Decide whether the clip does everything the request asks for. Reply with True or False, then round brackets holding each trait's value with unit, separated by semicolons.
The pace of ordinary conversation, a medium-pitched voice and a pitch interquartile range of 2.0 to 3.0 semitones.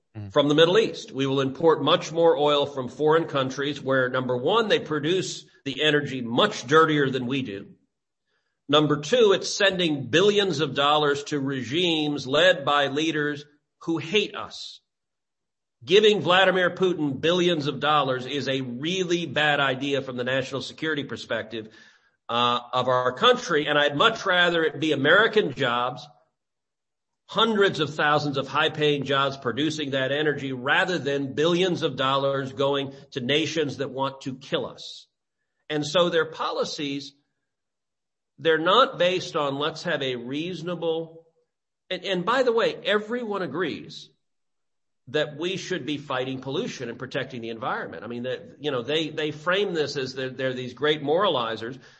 False (155 wpm; 150 Hz; 3.7 semitones)